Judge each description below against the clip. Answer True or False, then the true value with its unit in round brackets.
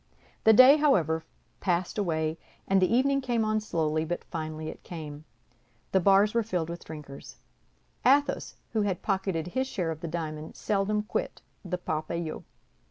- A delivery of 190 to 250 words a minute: False (160 wpm)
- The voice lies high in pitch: False (180 Hz)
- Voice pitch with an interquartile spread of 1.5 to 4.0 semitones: False (5.2 semitones)